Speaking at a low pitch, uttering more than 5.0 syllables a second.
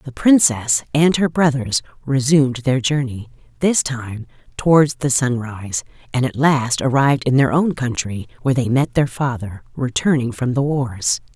No: low, 130 Hz; 4.6 syllables/s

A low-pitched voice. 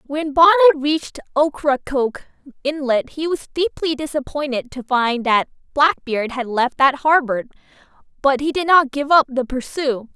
No: very high, 280 Hz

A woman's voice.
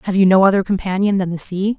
Yes: female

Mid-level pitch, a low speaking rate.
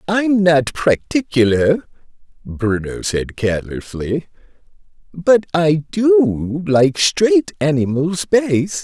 Yes: medium, 155 Hz; slow, 90 wpm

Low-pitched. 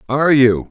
Yes: low, 130 Hz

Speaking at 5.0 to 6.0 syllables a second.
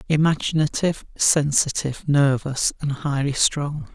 No: 4.5 syllables/s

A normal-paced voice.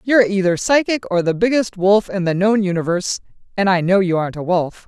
No: fast, 220 wpm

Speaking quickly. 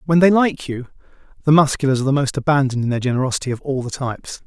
Yes: fast, 230 wpm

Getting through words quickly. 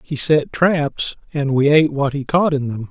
Yes: fast, 225 wpm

